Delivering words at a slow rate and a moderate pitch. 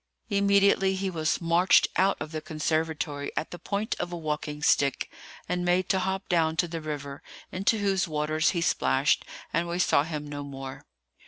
No: average, 180 wpm; medium, 165 Hz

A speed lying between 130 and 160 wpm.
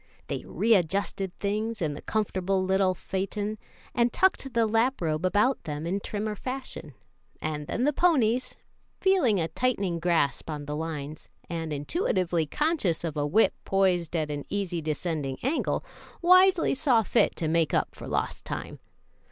Yes: average, 155 wpm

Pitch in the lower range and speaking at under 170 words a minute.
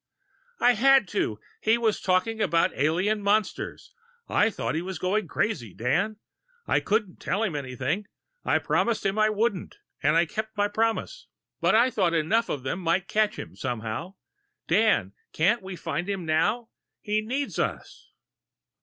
No: high, 200 Hz; average, 160 wpm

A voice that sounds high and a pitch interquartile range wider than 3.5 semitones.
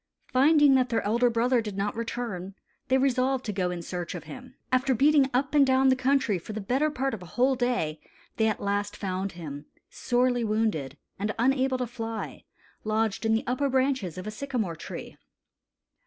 Yes: high, 235 Hz; average, 4.4 semitones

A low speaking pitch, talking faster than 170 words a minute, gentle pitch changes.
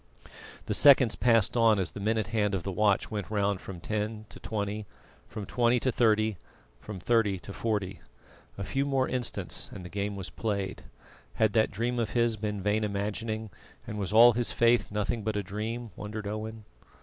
Yes: low, 105 Hz; average, 185 wpm; narrow, 2.2 semitones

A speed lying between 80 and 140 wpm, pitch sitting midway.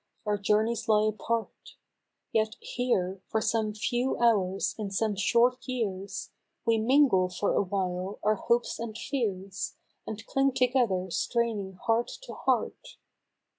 No: slow, 135 wpm; high, 215 Hz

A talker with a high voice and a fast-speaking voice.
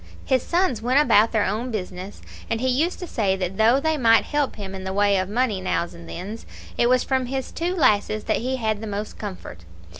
Yes: high, 220 Hz; fast, 230 wpm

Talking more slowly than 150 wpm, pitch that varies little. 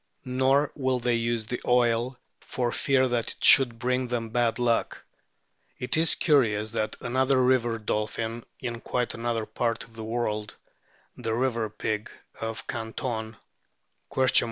Yes: average, 140 wpm; narrow, 2.0 semitones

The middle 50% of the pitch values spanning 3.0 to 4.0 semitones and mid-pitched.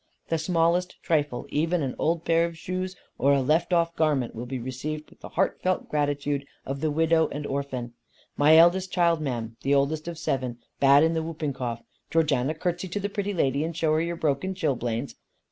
Yes: average, 3.3 semitones; medium, 155 Hz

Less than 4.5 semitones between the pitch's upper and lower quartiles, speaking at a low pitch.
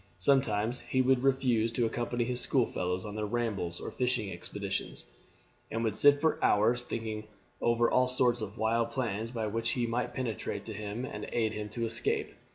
Yes: narrow, 2.4 semitones; low, 115 Hz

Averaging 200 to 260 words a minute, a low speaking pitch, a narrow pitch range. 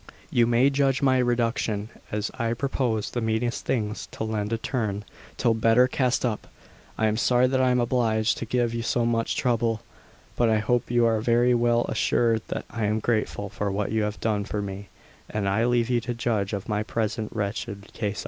Yes: fast, 205 wpm; low, 115 Hz; narrow, 2.2 semitones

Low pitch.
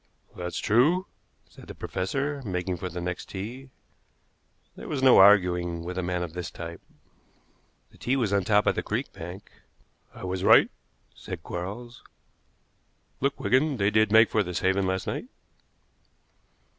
Yes: very low, 95 Hz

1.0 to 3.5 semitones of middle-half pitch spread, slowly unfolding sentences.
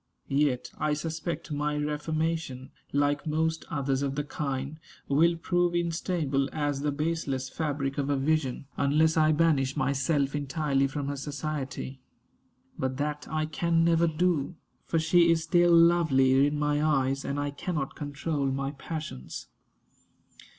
No: average, 2.7 semitones; average, 145 wpm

